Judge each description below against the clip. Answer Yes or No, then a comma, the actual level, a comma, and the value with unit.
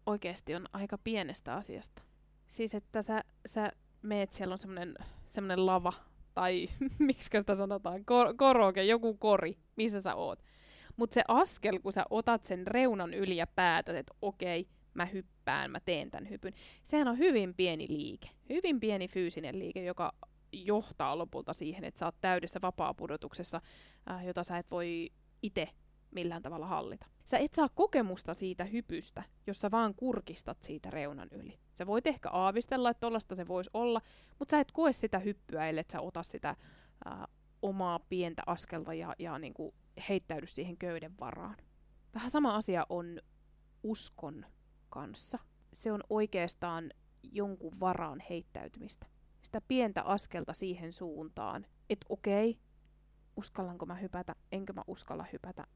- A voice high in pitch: Yes, high, 195 Hz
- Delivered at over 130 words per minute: Yes, average, 150 wpm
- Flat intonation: No, average, 4.2 semitones